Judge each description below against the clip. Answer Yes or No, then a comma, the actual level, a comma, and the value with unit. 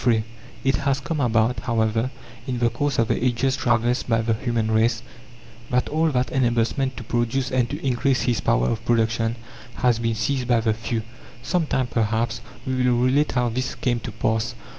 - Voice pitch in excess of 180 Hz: No, low, 120 Hz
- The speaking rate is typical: Yes, average, 195 wpm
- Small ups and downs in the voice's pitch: Yes, narrow, 2.3 semitones